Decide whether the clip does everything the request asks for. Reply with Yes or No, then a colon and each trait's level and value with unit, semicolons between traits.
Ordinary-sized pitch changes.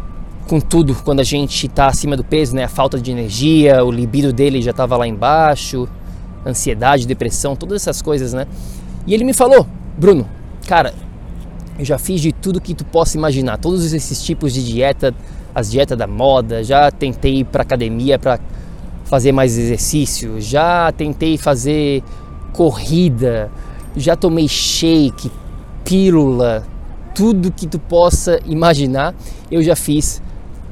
Yes: average, 4.3 semitones